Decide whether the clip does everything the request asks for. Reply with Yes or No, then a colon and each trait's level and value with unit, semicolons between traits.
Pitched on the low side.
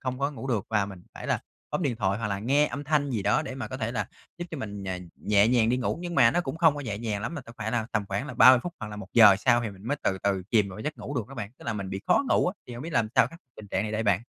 Yes: low, 115 Hz